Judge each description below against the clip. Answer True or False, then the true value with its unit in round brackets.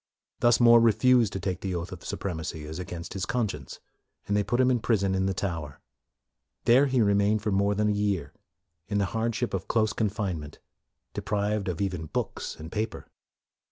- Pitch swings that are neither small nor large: True (3.5 semitones)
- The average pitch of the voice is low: True (100 Hz)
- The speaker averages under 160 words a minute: False (190 wpm)